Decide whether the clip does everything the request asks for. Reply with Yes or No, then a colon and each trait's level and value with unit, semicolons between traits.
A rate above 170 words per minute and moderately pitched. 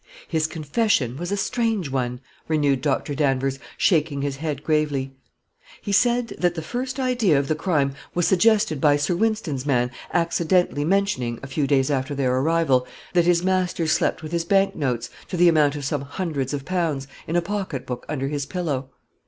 Yes: average, 180 wpm; medium, 155 Hz